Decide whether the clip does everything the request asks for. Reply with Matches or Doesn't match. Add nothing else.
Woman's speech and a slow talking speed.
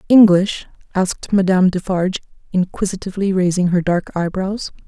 Matches